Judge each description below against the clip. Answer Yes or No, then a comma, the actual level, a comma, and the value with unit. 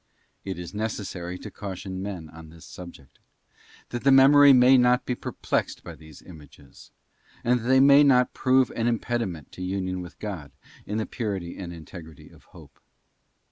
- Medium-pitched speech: No, low, 100 Hz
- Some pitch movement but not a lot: No, wide, 6.2 semitones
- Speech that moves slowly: No, average, 170 wpm